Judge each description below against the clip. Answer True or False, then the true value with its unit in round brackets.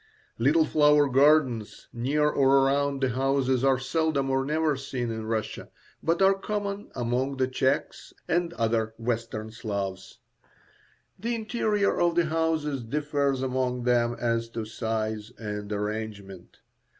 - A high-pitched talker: False (130 Hz)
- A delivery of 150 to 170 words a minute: False (135 wpm)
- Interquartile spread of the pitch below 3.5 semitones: False (4.8 semitones)